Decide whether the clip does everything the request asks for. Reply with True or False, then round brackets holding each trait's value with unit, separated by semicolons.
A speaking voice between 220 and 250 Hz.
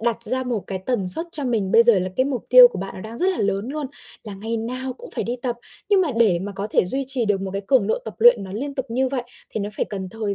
True (230 Hz)